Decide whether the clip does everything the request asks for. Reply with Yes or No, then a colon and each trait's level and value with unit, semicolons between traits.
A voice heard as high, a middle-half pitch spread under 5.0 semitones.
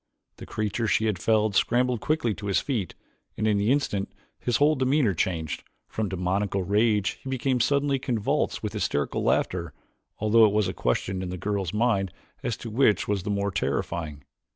No: low, 105 Hz; average, 3.9 semitones